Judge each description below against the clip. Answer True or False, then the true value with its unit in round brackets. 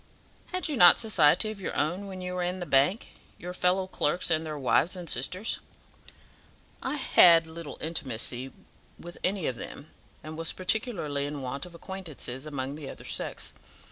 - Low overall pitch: False (170 Hz)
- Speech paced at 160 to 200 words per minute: True (170 wpm)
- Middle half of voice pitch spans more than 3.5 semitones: True (4.2 semitones)